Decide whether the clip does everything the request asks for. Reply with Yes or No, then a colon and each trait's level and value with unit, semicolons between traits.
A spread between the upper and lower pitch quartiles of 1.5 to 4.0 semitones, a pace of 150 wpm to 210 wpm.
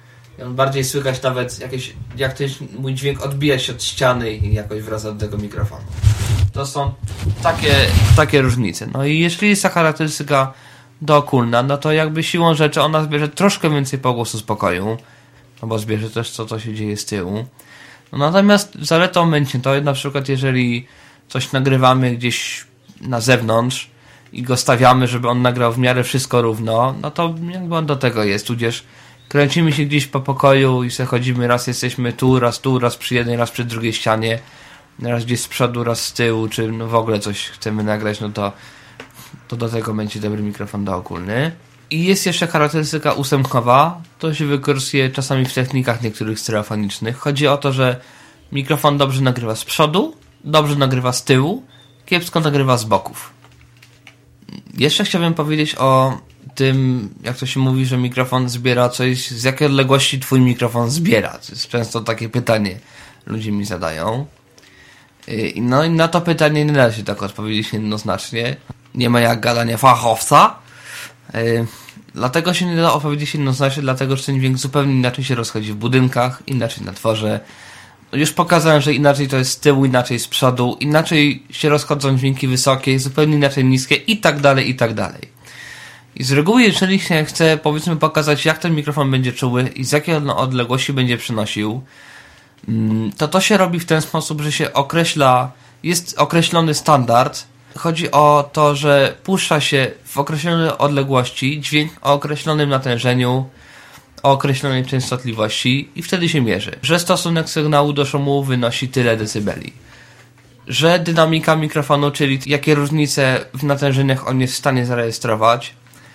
Yes: average, 3.6 semitones; fast, 160 wpm